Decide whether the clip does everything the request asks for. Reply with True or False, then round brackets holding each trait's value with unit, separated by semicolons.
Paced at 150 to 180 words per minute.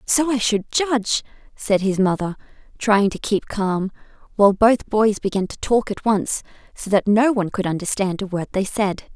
False (190 wpm)